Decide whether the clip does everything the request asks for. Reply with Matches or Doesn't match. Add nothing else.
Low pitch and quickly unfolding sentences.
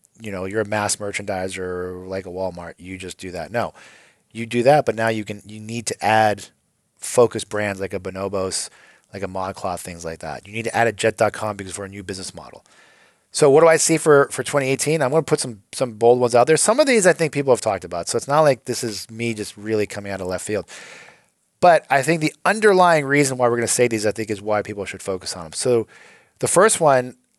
Matches